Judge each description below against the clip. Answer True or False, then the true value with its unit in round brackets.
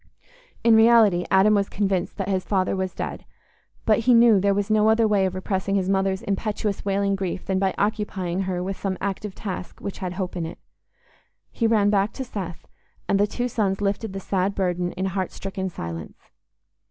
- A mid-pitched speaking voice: False (195 Hz)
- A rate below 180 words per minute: False (195 wpm)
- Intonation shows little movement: True (1.9 semitones)